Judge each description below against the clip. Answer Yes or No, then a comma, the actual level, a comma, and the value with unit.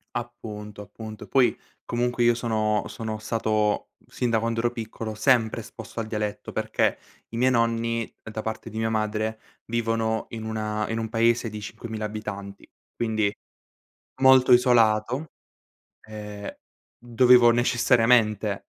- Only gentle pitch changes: Yes, narrow, 1.6 semitones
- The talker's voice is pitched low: Yes, low, 110 Hz